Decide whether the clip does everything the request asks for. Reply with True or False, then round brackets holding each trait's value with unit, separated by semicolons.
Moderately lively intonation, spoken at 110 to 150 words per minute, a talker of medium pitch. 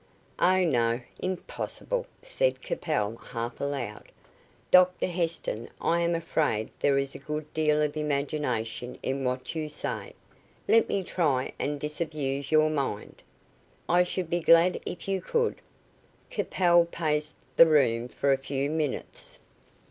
True (4.1 semitones; 135 wpm; 150 Hz)